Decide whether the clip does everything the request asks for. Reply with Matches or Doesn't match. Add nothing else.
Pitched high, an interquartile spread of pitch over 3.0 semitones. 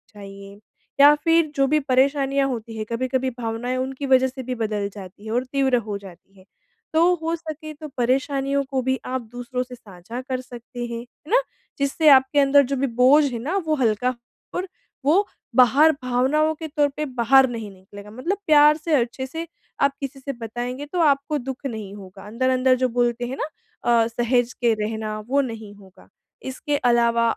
Matches